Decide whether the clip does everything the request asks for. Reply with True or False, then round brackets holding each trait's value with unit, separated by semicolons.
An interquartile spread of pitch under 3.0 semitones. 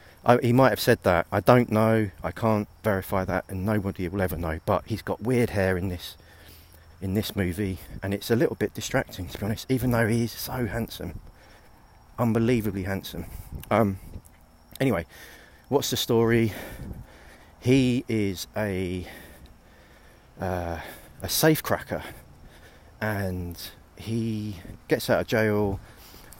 False (4.3 semitones)